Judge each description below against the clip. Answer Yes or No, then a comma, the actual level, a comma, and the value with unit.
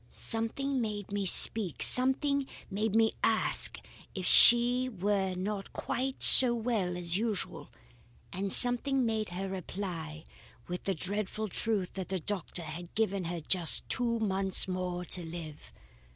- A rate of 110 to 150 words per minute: Yes, average, 140 wpm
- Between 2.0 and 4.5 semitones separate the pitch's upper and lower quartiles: Yes, average, 4.0 semitones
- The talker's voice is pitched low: No, high, 200 Hz